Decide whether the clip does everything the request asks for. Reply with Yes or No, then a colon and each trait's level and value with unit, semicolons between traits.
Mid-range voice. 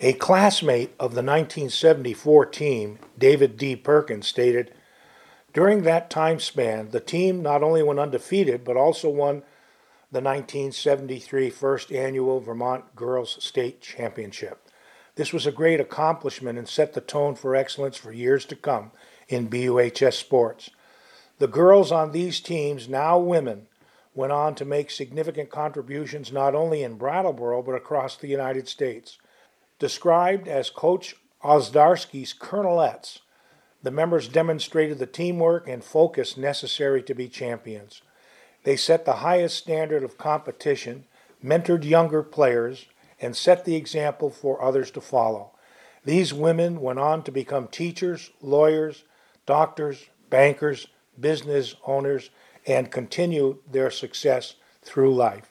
Yes: medium, 145 Hz